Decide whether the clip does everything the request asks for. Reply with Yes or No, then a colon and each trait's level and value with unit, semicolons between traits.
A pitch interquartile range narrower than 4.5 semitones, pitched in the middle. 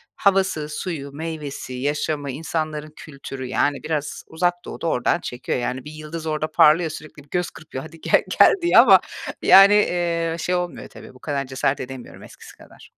Yes: average, 3.2 semitones; medium, 155 Hz